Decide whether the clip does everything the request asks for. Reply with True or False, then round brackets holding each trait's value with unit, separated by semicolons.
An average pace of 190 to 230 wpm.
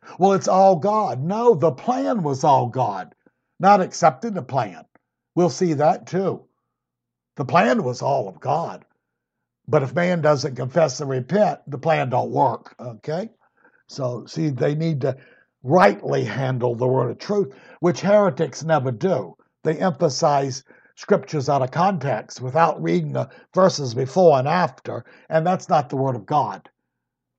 False (155 wpm)